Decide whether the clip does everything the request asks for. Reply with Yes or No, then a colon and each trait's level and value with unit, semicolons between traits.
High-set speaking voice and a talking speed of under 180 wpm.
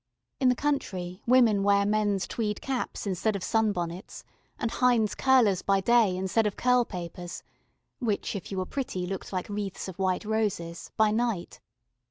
Yes: high, 205 Hz; average, 165 wpm